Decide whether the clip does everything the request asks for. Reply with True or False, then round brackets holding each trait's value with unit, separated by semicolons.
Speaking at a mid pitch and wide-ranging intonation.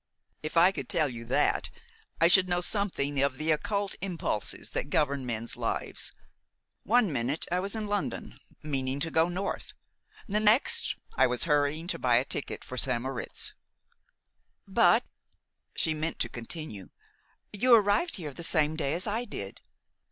True (160 Hz; 6.4 semitones)